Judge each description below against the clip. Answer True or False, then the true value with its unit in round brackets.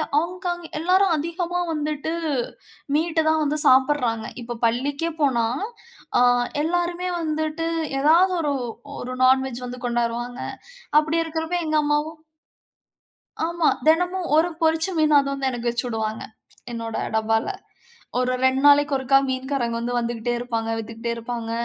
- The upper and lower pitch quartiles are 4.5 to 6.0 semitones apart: True (5.1 semitones)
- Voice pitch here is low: False (285 Hz)